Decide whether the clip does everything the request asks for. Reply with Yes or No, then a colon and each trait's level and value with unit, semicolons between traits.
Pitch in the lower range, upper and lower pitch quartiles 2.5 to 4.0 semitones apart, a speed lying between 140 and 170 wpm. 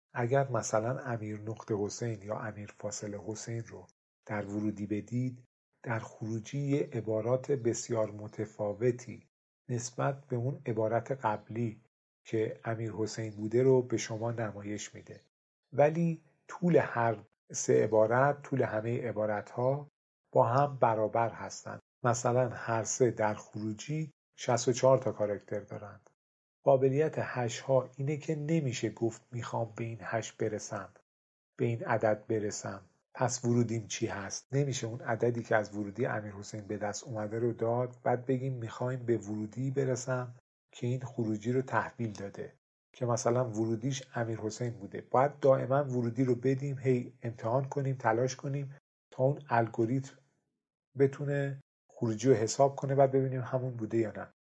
Yes: low, 120 Hz; average, 3.3 semitones; average, 145 wpm